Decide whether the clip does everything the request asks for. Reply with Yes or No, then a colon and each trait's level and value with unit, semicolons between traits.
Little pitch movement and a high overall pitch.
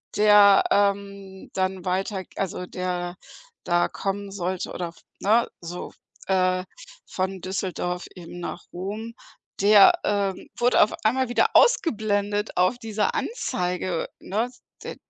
Yes: narrow, 2.3 semitones; high, 195 Hz